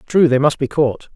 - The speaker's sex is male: Yes, male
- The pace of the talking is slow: No, fast, 260 wpm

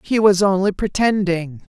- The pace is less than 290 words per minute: Yes, slow, 135 wpm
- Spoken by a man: No, female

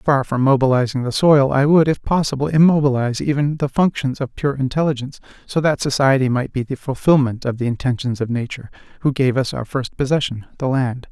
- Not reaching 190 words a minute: No, average, 195 wpm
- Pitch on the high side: No, low, 135 Hz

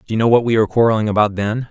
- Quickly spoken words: Yes, fast, 315 wpm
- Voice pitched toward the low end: Yes, low, 110 Hz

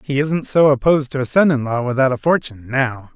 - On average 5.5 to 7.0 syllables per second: Yes, 6.0 syllables/s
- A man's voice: Yes, male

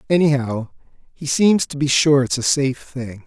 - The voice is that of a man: Yes, male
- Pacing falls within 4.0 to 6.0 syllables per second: Yes, 4.9 syllables/s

